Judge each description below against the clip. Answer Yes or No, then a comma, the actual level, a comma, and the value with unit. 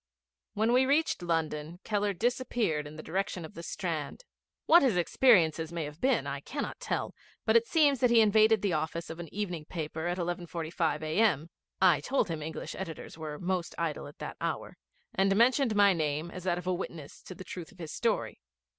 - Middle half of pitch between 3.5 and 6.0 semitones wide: Yes, average, 4.9 semitones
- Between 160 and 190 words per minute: No, average, 200 wpm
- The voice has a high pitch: No, medium, 175 Hz